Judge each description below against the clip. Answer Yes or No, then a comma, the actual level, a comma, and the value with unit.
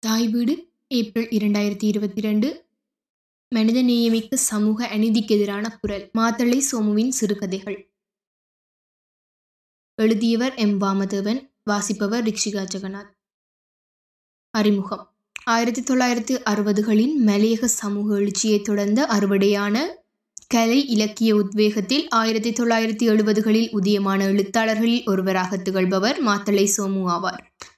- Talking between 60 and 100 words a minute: Yes, average, 95 wpm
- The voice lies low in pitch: No, high, 215 Hz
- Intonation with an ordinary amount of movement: No, narrow, 2.2 semitones